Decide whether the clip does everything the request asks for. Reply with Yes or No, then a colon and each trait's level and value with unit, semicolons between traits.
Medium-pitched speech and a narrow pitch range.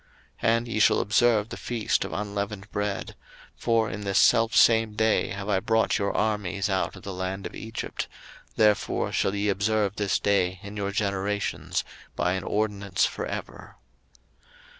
No: low, 105 Hz; narrow, 1.8 semitones